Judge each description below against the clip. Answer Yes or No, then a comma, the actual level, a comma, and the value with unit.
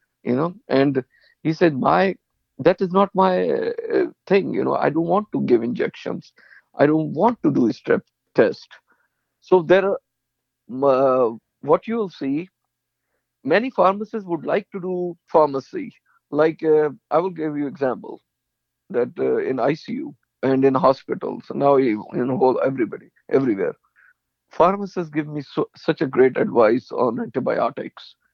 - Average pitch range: No, wide, 6.1 semitones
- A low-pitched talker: No, medium, 165 Hz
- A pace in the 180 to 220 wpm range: No, average, 155 wpm